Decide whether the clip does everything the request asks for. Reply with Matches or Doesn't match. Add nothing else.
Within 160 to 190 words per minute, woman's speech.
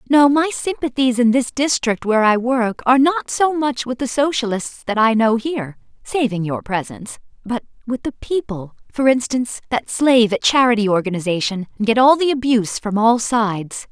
Matches